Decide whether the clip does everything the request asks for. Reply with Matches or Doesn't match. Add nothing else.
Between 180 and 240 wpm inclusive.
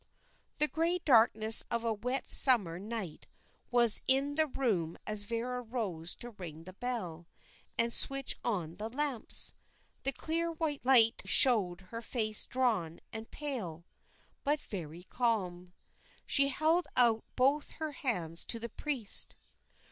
Doesn't match